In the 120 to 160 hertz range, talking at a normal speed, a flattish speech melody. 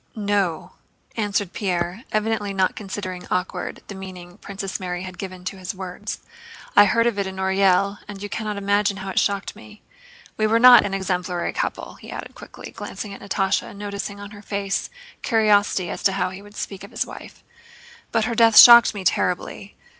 No: high, 200 Hz; average, 190 wpm; narrow, 1.7 semitones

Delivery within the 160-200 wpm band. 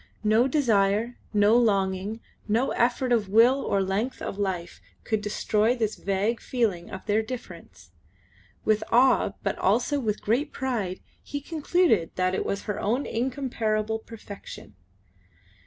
No: average, 140 wpm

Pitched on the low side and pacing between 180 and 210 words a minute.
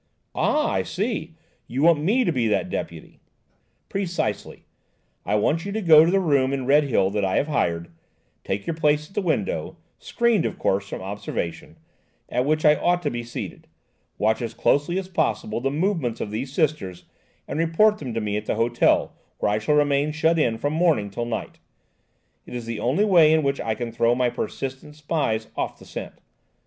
No: medium, 145 Hz; average, 185 wpm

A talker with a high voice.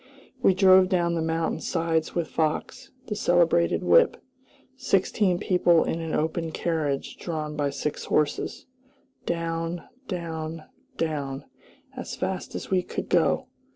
No: medium, 165 Hz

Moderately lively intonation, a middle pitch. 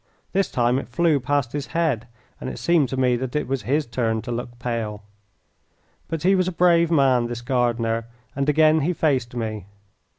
No: average, 4.6 semitones; low, 130 Hz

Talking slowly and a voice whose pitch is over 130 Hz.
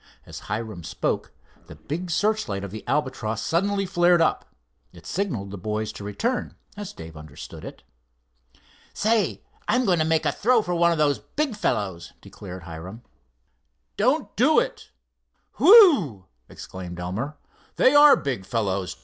No: average, 150 wpm; medium, 140 Hz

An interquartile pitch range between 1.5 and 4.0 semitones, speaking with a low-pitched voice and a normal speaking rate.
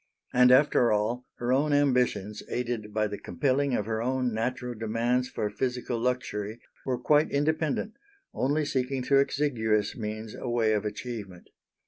Yes: average, 3.3 semitones; low, 125 Hz; average, 150 wpm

